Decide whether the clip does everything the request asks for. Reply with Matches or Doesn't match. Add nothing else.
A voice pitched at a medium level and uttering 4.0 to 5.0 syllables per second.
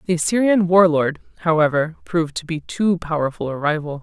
Doesn't match